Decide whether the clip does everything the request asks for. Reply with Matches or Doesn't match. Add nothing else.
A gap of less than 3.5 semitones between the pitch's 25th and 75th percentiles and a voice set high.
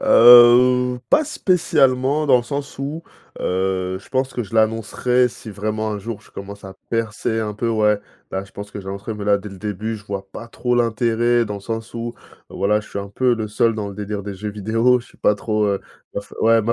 Doesn't match